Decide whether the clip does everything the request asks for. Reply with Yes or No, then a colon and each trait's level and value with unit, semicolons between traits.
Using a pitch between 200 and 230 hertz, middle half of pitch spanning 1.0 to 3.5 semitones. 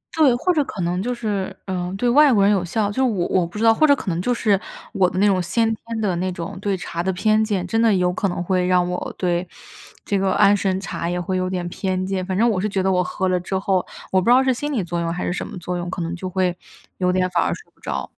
No: high, 190 Hz; average, 3.1 semitones